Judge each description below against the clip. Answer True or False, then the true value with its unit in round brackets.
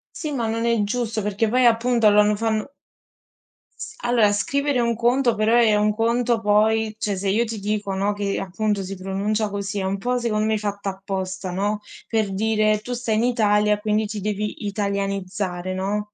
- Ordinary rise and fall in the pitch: False (2.1 semitones)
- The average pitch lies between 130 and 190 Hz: False (210 Hz)